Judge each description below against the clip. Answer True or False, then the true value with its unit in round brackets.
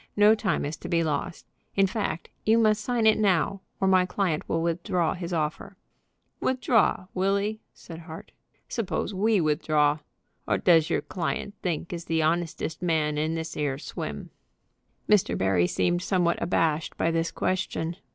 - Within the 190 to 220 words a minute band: False (165 wpm)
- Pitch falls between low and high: True (170 Hz)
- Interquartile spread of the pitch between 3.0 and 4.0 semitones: True (3.5 semitones)